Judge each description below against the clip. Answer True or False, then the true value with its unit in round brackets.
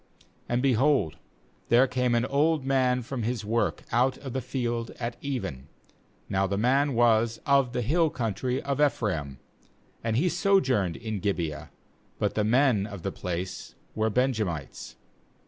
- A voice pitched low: True (120 Hz)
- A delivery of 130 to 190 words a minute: True (150 wpm)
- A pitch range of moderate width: True (4.2 semitones)